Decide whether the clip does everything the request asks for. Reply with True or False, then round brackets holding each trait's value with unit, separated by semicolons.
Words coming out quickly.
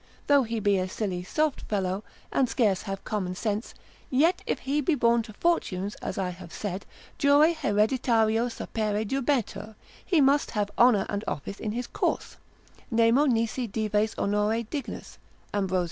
False (160 wpm)